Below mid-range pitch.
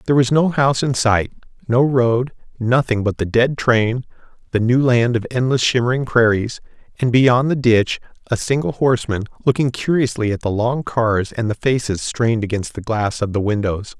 Yes: low, 120 Hz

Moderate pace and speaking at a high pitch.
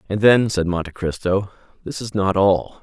No: average, 190 wpm; very low, 95 Hz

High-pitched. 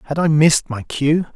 No: medium, 150 Hz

